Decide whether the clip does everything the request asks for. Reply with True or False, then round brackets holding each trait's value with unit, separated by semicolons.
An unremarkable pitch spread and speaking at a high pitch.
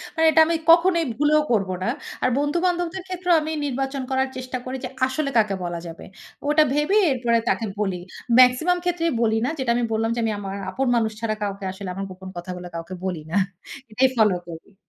False (7.5 semitones; 255 Hz)